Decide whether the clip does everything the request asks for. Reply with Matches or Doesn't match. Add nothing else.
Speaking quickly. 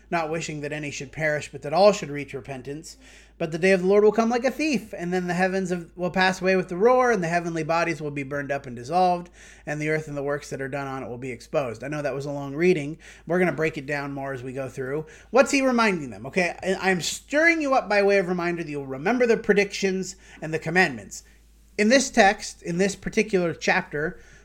Matches